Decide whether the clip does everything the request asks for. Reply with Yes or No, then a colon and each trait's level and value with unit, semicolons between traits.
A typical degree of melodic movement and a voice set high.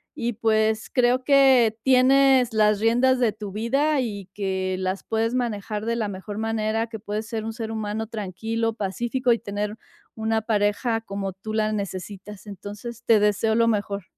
No: narrow, 2.2 semitones; high, 220 Hz